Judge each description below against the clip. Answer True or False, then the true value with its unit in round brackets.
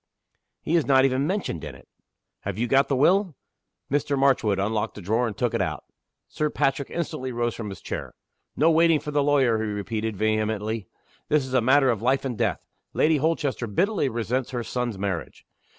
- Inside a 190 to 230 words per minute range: True (195 wpm)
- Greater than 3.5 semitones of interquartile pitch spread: True (4.7 semitones)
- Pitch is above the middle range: False (125 Hz)